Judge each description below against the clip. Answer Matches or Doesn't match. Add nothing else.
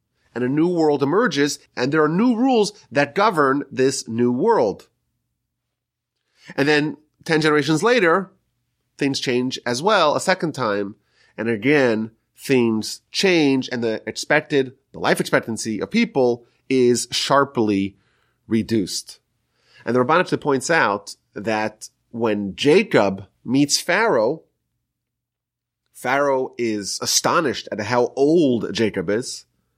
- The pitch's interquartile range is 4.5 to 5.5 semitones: Matches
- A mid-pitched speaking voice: Doesn't match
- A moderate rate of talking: Doesn't match